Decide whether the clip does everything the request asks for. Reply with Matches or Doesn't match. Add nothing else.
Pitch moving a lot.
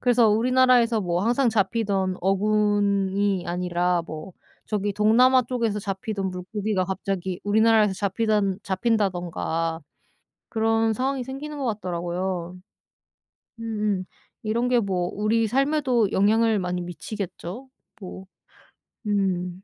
Doesn't match